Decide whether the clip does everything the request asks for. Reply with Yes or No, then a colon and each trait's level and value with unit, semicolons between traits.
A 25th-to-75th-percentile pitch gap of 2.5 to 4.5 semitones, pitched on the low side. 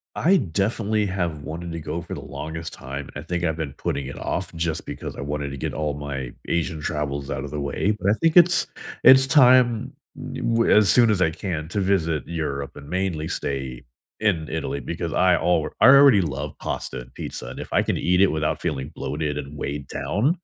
No: wide, 5.5 semitones; very low, 80 Hz